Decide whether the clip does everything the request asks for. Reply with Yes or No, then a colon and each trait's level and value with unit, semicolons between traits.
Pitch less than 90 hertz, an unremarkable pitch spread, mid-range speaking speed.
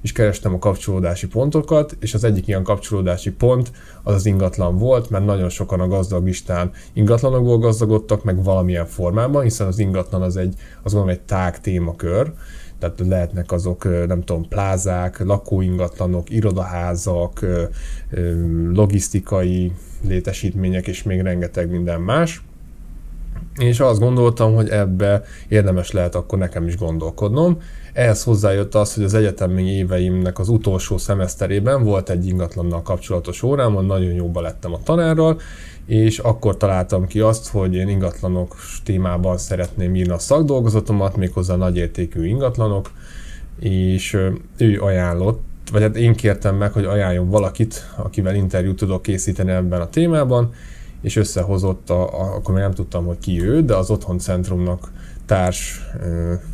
No: very low, 95 Hz; average, 3.0 semitones; average, 135 wpm